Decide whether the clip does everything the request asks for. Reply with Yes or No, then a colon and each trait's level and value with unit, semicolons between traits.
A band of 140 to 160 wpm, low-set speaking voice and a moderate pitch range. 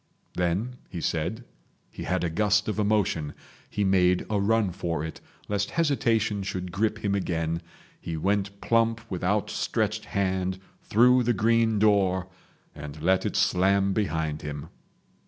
Yes: average, 145 wpm; low, 100 Hz; average, 3.4 semitones